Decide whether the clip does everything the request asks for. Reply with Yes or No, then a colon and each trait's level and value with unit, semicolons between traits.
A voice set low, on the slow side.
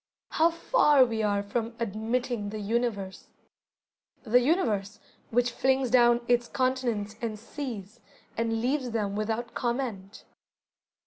No: high, 235 Hz; slow, 120 wpm